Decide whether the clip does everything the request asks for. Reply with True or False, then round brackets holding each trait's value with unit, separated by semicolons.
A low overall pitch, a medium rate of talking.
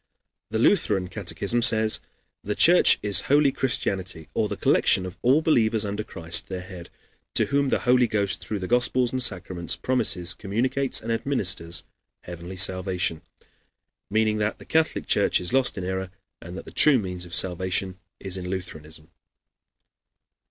True (100 Hz; 160 wpm)